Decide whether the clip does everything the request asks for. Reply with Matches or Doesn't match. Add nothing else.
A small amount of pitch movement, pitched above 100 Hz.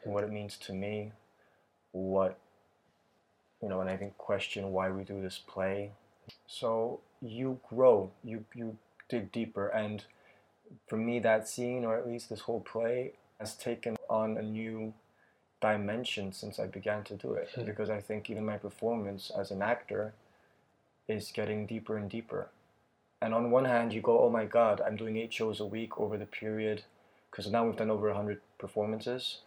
Matches